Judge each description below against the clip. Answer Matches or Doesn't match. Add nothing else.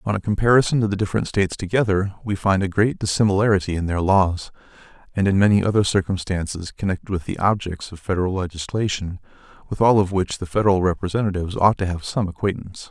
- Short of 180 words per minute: Doesn't match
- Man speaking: Matches